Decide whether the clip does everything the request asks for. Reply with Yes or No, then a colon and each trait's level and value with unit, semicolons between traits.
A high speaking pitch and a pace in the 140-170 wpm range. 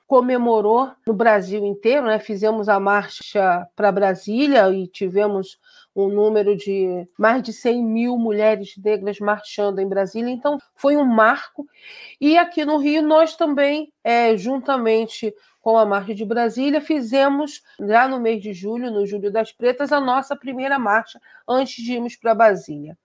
Yes: high, 225 Hz; average, 155 wpm